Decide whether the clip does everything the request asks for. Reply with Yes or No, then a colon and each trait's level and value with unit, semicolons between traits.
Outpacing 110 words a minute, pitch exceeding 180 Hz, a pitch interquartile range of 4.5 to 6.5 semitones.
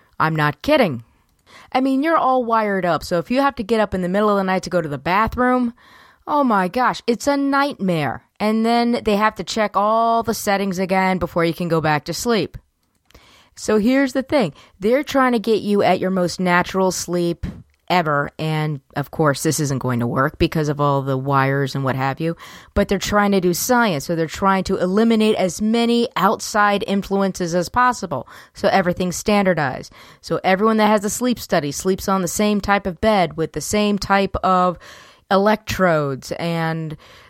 Yes: average, 200 wpm; high, 190 Hz; average, 5.0 semitones